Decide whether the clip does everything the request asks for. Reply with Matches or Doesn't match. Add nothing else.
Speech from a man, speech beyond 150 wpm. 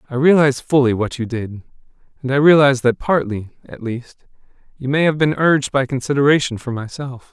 Matches